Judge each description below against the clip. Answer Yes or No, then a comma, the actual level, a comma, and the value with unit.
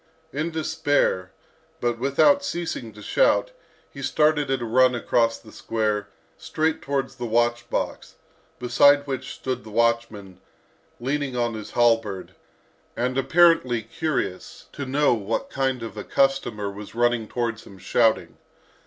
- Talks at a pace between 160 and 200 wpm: No, average, 140 wpm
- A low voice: Yes, low, 120 Hz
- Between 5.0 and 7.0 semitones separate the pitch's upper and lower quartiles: No, average, 3.6 semitones